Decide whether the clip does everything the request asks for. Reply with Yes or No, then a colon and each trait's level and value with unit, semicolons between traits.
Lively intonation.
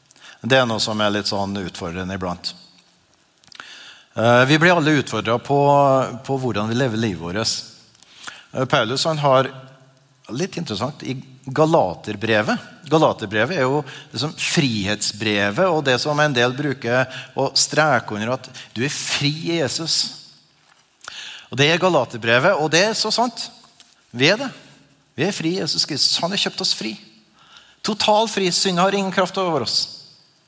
Yes: wide, 6.2 semitones